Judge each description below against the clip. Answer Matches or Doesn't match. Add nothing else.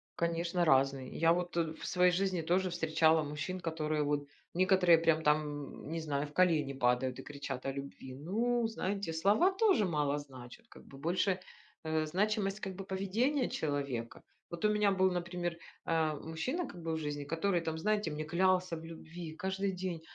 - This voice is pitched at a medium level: Matches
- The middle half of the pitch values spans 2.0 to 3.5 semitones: Doesn't match